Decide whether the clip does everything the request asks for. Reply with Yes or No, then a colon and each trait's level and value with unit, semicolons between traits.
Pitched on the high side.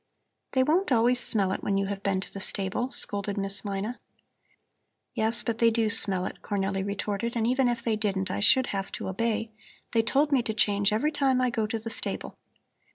Yes: high, 220 Hz